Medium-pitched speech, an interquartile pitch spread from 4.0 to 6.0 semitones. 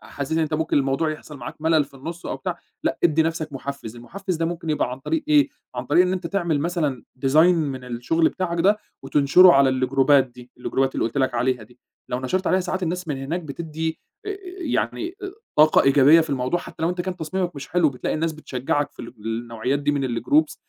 Yes: medium, 155 Hz; average, 4.5 semitones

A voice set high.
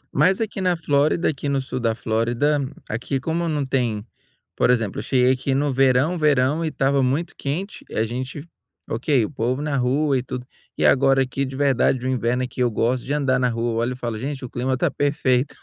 No: low, 130 Hz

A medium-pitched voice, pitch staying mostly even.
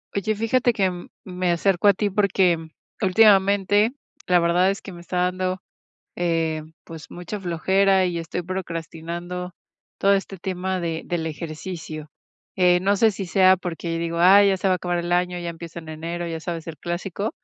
Yes: medium, 180 Hz; narrow, 2.3 semitones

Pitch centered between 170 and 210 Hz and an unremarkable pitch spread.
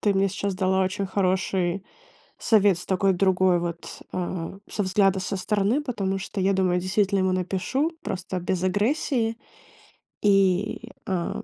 No: high, 190 Hz; narrow, 1.6 semitones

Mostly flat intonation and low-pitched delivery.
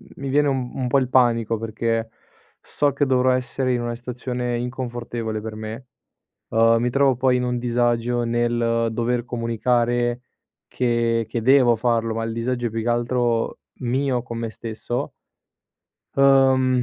Yes: narrow, 1.6 semitones; low, 120 Hz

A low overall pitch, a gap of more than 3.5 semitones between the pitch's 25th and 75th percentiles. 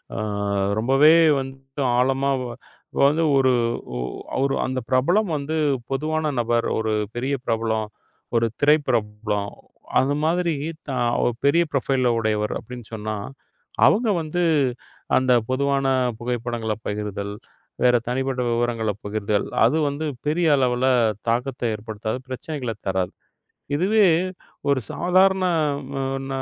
Yes: low, 130 Hz; average, 4.3 semitones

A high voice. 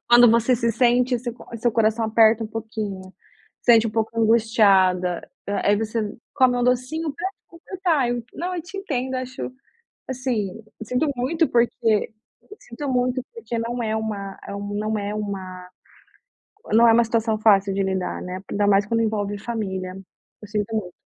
Yes: high, 225 Hz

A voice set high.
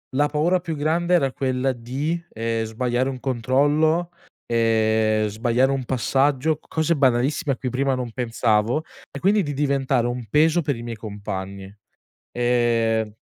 No: low, 130 Hz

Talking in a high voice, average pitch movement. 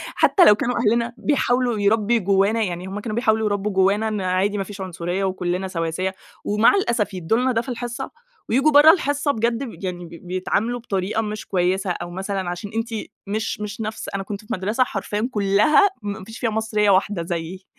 Yes: high, 210 Hz; average, 3.5 semitones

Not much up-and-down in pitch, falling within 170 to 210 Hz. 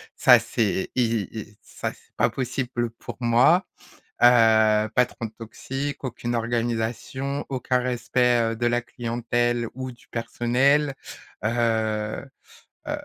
No: narrow, 1.9 semitones; low, 120 Hz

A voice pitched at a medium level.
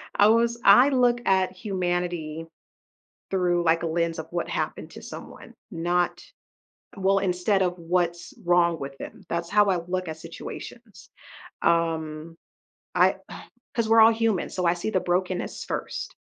Yes: medium, 180 Hz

